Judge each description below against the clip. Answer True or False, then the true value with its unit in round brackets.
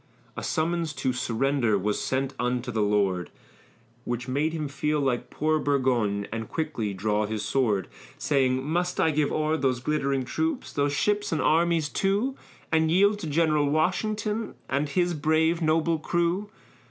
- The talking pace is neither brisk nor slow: True (155 wpm)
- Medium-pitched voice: True (150 Hz)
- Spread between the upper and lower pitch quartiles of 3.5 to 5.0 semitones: True (4.7 semitones)